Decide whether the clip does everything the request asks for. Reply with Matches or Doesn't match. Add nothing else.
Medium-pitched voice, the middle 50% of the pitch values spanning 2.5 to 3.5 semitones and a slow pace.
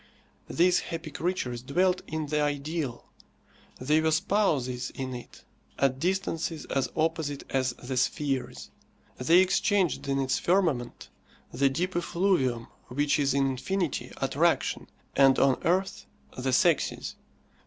Doesn't match